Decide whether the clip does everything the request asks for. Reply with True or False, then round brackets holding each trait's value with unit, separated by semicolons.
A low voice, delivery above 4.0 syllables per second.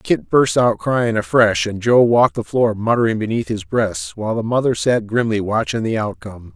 True (115 Hz; 5.1 syllables/s)